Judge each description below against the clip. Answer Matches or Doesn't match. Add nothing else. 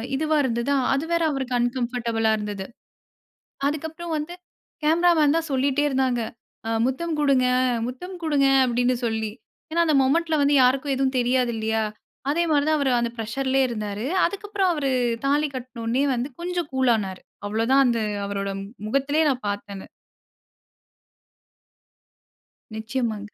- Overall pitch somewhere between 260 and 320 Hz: Matches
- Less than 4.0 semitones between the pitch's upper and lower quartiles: Doesn't match